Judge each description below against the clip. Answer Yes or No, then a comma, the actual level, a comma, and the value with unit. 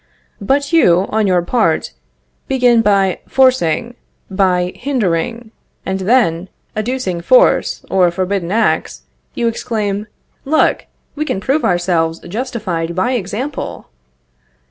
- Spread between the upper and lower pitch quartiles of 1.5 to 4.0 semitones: No, wide, 5.6 semitones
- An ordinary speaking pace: No, slow, 110 wpm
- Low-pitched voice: No, high, 205 Hz